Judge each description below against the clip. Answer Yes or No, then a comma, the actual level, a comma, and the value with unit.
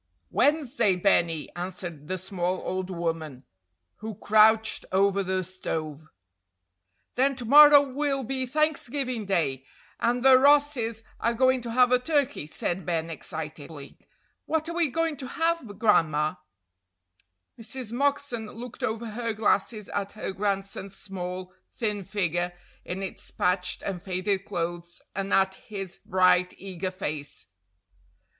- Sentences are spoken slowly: Yes, slow, 130 wpm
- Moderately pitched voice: No, high, 200 Hz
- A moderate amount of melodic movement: No, wide, 5.7 semitones